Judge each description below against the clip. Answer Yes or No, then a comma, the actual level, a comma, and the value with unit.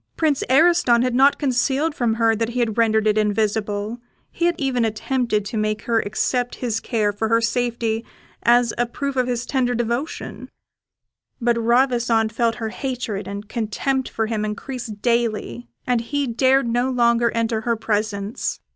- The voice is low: No, high, 235 Hz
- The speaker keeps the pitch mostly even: Yes, narrow, 2.3 semitones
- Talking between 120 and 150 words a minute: No, average, 165 wpm